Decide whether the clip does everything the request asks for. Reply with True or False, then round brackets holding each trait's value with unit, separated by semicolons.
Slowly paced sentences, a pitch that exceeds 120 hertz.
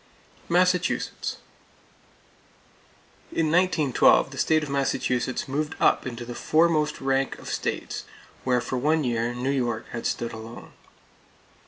True (125 wpm; 135 Hz)